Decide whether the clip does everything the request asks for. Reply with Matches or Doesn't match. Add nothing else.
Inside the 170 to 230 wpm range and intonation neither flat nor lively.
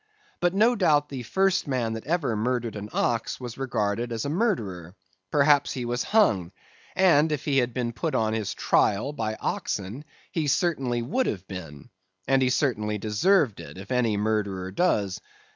Doesn't match